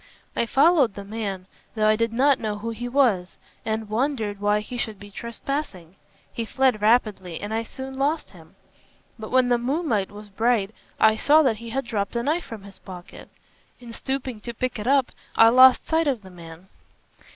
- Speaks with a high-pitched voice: Yes, high, 225 Hz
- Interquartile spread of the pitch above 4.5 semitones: No, average, 3.9 semitones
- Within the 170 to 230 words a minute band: Yes, average, 195 wpm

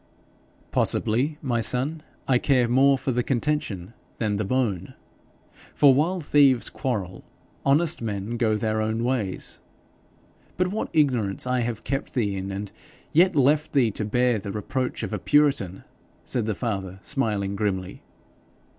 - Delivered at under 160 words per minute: Yes, average, 145 wpm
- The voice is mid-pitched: No, low, 120 Hz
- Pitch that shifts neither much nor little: Yes, average, 4.9 semitones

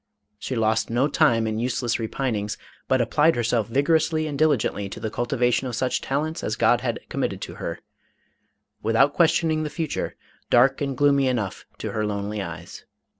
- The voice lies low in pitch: Yes, low, 125 Hz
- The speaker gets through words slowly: No, average, 170 wpm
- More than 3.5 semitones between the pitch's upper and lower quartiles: Yes, average, 4.5 semitones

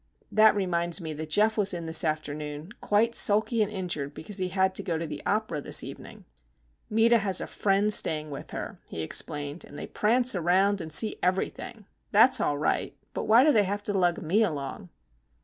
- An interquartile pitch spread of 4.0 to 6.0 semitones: Yes, average, 5.2 semitones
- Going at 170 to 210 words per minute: Yes, average, 200 wpm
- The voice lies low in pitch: No, high, 190 Hz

